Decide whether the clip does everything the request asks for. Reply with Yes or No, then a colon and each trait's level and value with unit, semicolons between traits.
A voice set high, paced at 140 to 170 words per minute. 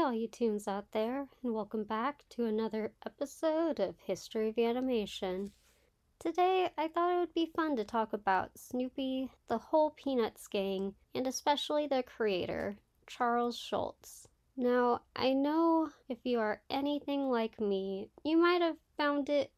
Yes: high, 245 Hz; average, 155 wpm